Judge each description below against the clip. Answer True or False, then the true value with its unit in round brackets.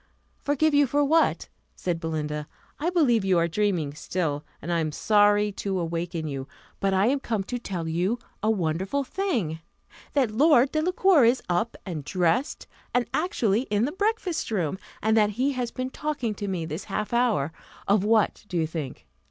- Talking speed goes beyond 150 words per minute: True (180 wpm)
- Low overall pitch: False (205 Hz)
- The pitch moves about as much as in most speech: False (7.3 semitones)